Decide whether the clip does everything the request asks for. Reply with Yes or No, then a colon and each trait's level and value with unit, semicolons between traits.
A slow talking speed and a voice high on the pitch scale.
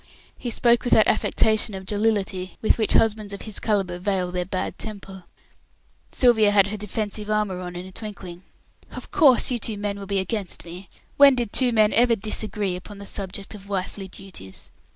No: average, 190 wpm; high, 205 Hz